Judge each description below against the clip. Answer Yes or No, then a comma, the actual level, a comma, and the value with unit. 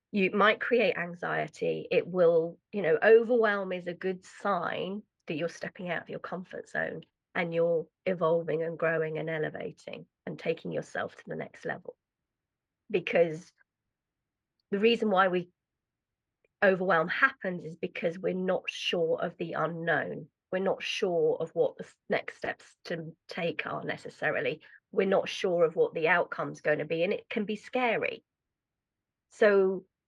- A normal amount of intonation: No, wide, 6.5 semitones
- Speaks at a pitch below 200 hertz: Yes, high, 190 Hz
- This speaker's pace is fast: No, average, 155 wpm